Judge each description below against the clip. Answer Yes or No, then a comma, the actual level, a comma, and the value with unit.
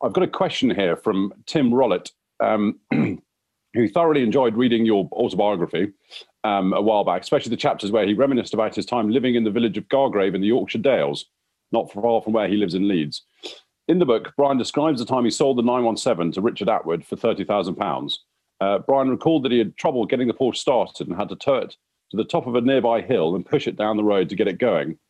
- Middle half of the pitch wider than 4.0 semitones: No, average, 3.6 semitones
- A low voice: Yes, low, 120 Hz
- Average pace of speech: No, fast, 235 wpm